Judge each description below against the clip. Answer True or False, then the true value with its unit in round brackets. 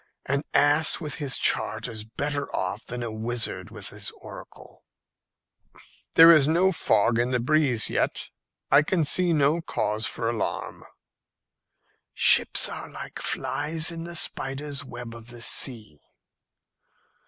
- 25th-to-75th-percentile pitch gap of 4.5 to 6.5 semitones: True (4.9 semitones)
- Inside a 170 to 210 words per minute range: False (140 wpm)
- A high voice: False (140 Hz)